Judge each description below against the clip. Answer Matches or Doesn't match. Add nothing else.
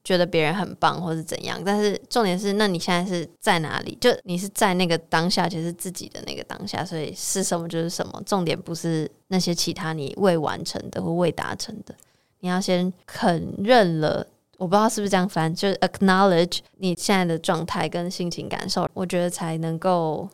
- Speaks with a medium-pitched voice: Matches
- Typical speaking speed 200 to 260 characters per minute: Doesn't match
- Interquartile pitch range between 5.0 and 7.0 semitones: Doesn't match